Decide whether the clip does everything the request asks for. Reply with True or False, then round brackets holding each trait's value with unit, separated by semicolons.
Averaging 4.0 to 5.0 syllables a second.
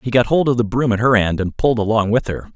False (6.6 syllables/s)